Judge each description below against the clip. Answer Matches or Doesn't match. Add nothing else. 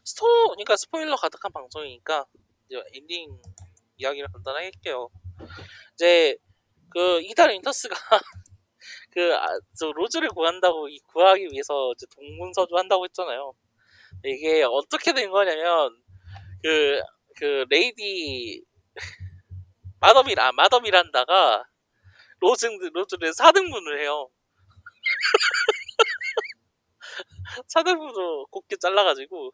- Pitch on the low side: Doesn't match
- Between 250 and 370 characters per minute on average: Doesn't match